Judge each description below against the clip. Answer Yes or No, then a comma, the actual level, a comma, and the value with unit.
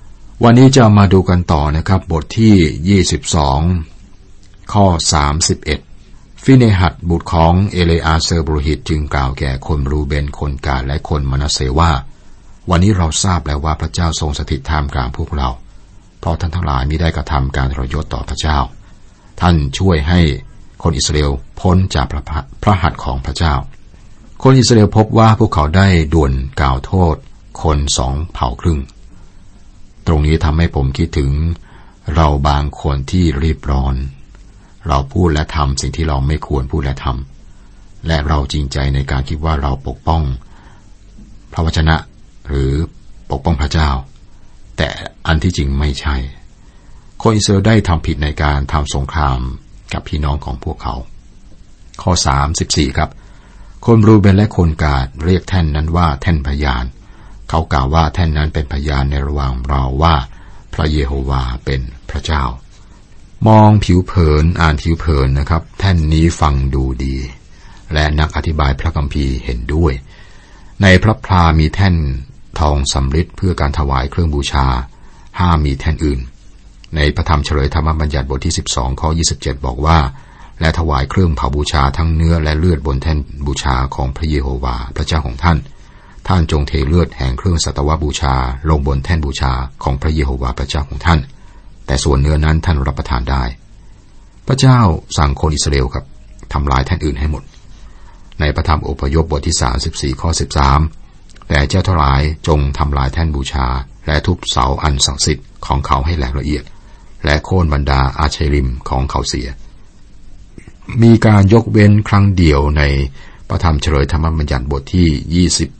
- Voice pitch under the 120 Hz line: Yes, very low, 80 Hz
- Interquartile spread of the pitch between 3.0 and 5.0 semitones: Yes, average, 4.3 semitones